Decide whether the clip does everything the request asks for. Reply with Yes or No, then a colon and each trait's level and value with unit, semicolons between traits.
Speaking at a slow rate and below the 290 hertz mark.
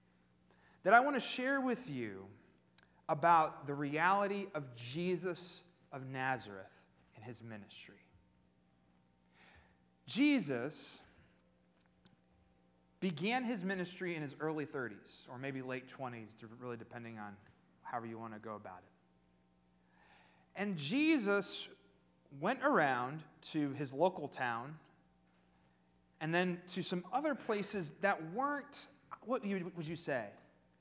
Yes: slow, 115 wpm; low, 135 Hz